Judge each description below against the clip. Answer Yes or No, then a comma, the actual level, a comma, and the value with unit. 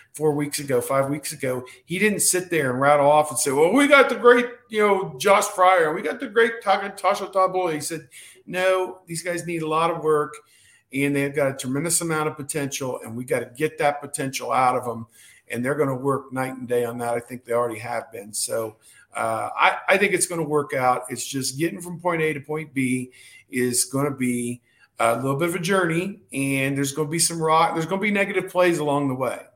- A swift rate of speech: Yes, fast, 245 wpm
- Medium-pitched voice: Yes, medium, 150 Hz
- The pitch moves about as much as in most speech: No, wide, 5.7 semitones